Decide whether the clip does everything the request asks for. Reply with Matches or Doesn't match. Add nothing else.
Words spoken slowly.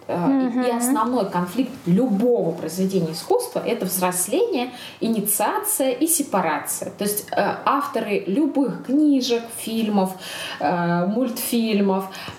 Matches